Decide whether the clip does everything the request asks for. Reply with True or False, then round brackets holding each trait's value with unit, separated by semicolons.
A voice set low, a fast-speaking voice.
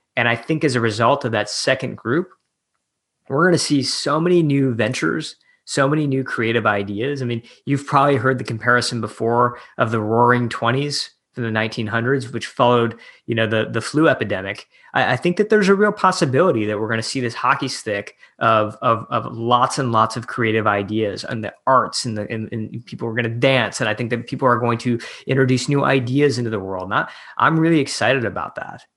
True (120 Hz; 215 wpm)